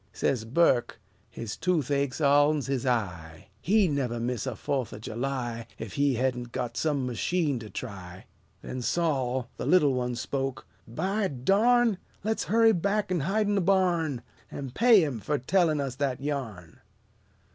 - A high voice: No, low, 135 Hz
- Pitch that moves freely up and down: Yes, wide, 6.2 semitones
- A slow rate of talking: No, average, 155 wpm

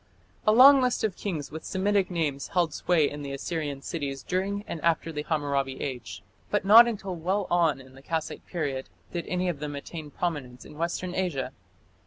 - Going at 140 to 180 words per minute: No, average, 190 wpm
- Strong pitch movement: No, average, 4.5 semitones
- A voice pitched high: No, medium, 165 Hz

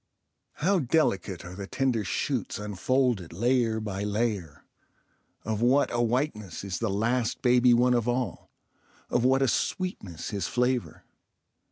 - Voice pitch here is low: Yes, low, 120 Hz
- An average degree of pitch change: Yes, average, 3.8 semitones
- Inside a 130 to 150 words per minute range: Yes, average, 140 wpm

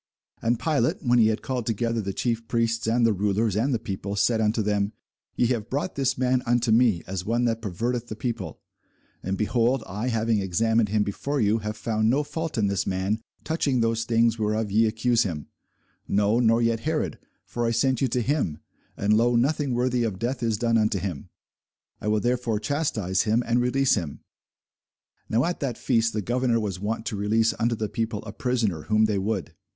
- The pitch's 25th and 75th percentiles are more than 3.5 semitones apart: No, narrow, 2.5 semitones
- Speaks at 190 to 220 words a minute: Yes, average, 200 wpm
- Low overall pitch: Yes, low, 115 Hz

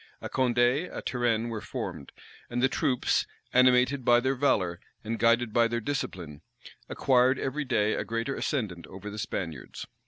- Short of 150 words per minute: No, average, 160 wpm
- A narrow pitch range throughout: No, average, 3.2 semitones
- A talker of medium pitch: No, low, 120 Hz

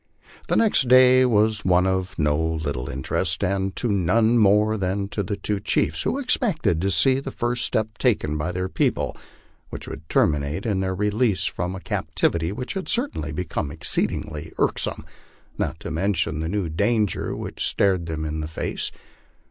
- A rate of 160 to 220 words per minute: Yes, average, 170 wpm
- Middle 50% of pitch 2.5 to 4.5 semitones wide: No, average, 5.3 semitones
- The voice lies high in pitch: No, very low, 95 Hz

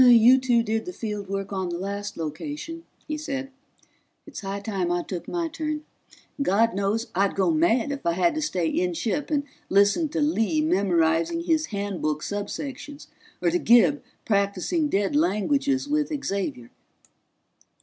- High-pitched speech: Yes, high, 225 Hz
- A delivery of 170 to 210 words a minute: No, average, 160 wpm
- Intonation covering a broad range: Yes, wide, 7.1 semitones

